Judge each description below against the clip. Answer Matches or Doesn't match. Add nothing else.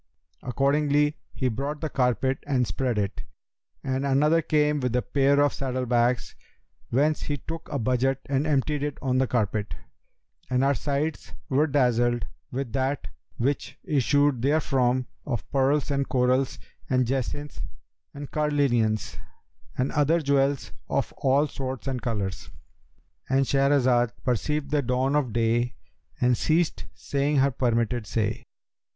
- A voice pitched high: Doesn't match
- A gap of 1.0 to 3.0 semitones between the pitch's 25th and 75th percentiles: Matches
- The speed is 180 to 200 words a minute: Doesn't match